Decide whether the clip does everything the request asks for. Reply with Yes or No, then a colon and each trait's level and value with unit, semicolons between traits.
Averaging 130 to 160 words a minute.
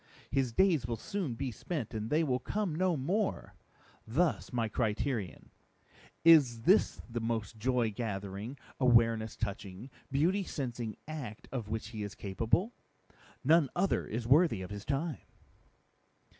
Yes: average, 140 wpm